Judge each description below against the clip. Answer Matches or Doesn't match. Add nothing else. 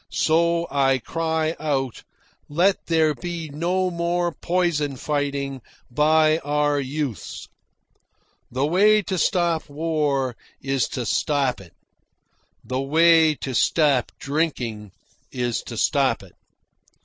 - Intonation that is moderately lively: Matches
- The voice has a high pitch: Doesn't match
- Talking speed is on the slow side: Matches